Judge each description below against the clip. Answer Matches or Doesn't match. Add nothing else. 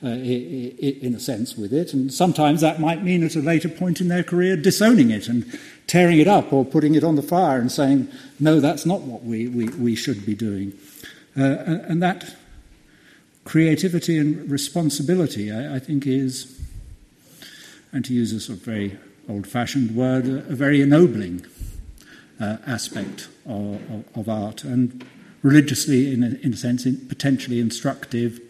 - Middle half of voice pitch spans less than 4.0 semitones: Doesn't match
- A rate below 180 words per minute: Matches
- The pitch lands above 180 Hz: Doesn't match